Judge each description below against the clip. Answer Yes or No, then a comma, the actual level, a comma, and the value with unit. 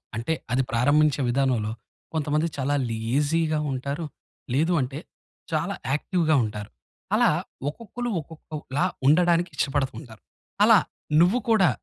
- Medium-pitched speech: Yes, medium, 150 Hz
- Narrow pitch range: No, average, 3.9 semitones